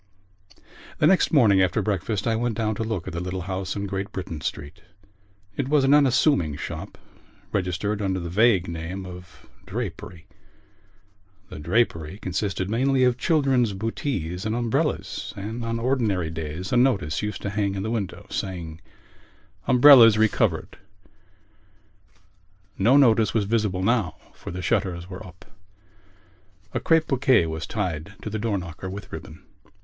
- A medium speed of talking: Yes, average, 155 wpm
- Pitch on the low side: Yes, low, 100 Hz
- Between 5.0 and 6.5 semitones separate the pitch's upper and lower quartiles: No, average, 4.4 semitones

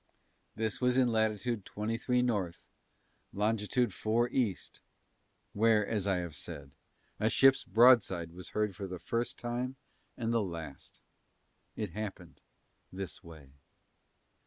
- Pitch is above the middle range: No, low, 105 Hz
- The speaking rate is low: Yes, slow, 125 wpm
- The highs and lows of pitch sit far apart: No, average, 4.4 semitones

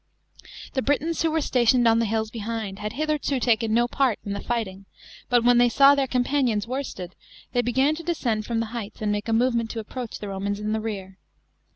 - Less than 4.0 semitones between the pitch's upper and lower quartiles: Yes, average, 3.3 semitones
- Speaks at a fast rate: Yes, fast, 225 wpm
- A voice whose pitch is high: Yes, high, 230 Hz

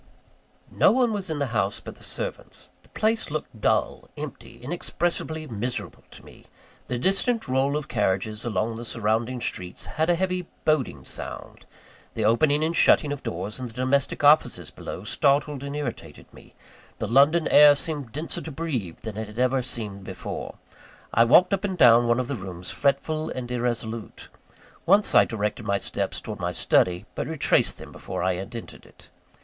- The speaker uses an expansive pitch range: Yes, wide, 5.7 semitones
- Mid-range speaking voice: No, low, 130 Hz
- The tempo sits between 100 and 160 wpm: No, average, 180 wpm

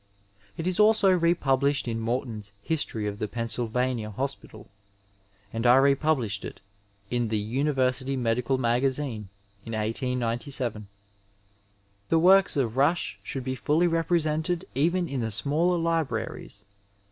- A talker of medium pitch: No, low, 130 Hz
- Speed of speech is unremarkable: No, slow, 125 wpm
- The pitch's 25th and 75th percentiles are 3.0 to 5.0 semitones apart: No, wide, 5.6 semitones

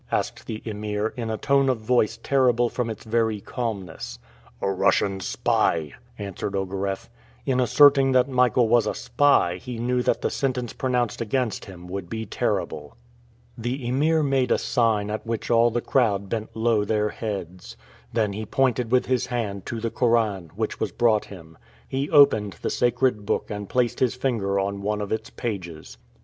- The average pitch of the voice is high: No, low, 115 Hz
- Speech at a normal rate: Yes, average, 175 wpm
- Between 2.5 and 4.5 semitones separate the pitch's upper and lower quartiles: Yes, average, 3.7 semitones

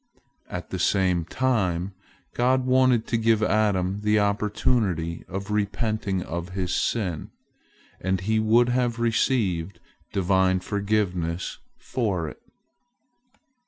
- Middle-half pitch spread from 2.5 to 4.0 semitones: Yes, average, 3.5 semitones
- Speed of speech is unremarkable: No, slow, 110 wpm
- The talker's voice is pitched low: Yes, low, 100 Hz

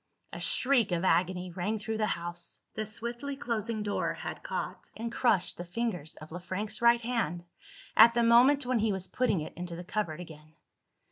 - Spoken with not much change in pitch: No, average, 5.0 semitones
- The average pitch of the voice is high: Yes, high, 210 Hz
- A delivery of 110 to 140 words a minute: No, average, 190 wpm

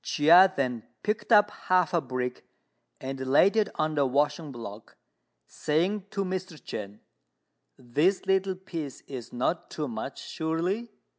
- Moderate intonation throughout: No, wide, 6.1 semitones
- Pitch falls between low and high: Yes, medium, 160 Hz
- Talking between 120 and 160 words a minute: Yes, average, 140 wpm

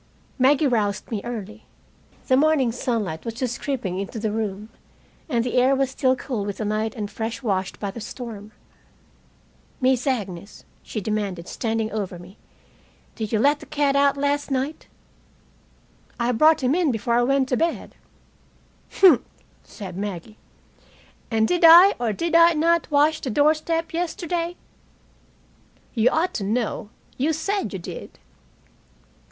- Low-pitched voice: No, high, 245 Hz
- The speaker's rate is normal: Yes, average, 150 wpm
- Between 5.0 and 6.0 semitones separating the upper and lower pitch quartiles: Yes, wide, 5.5 semitones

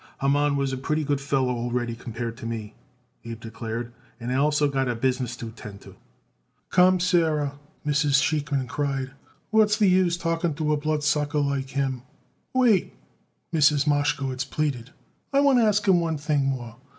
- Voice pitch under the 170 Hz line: Yes, medium, 140 Hz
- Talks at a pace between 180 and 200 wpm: No, average, 165 wpm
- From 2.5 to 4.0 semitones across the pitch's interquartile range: Yes, average, 3.5 semitones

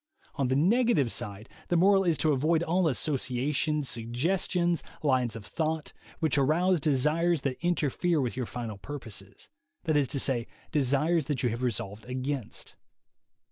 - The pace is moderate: Yes, average, 150 wpm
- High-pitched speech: No, medium, 145 Hz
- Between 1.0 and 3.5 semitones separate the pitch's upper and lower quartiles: No, average, 4.8 semitones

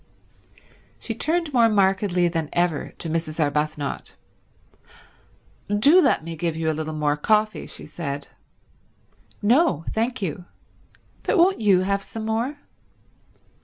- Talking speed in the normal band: No, slow, 130 wpm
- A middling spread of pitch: No, wide, 6.1 semitones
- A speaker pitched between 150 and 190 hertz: Yes, medium, 185 Hz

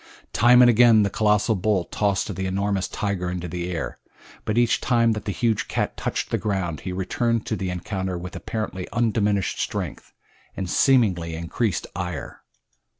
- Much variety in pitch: No, average, 3.6 semitones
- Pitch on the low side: Yes, low, 100 Hz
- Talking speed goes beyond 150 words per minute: Yes, average, 170 wpm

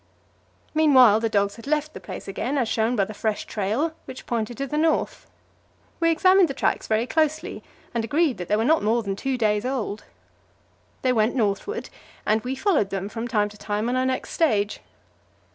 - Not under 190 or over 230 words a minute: Yes, average, 195 wpm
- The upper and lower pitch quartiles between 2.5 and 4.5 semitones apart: No, average, 5.2 semitones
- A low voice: No, high, 235 Hz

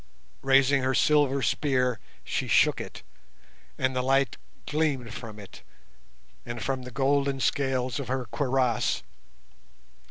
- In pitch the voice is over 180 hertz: No, low, 130 Hz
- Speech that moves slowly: Yes, slow, 125 wpm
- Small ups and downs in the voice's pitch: Yes, narrow, 1.7 semitones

